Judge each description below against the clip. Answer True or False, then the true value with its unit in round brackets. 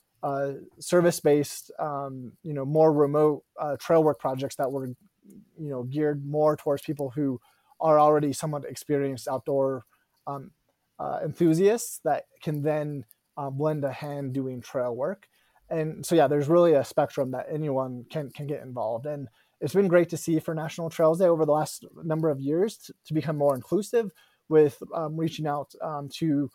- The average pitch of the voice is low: False (150 Hz)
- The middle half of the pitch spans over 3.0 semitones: False (2.5 semitones)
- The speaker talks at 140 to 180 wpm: True (175 wpm)